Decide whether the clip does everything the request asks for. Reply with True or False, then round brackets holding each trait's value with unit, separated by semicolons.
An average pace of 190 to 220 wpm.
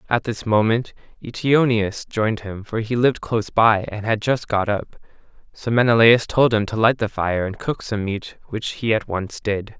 True (200 wpm)